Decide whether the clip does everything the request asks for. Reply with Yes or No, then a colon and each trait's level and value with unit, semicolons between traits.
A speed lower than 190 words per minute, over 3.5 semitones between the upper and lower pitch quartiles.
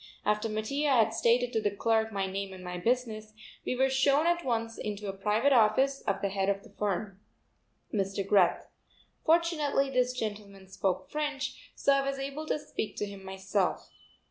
Yes: average, 180 wpm; wide, 5.4 semitones